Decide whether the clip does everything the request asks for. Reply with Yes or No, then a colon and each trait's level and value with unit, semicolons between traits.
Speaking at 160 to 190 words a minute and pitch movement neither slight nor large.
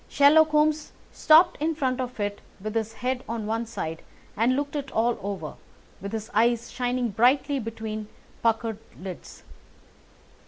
No: average, 150 wpm; average, 4.1 semitones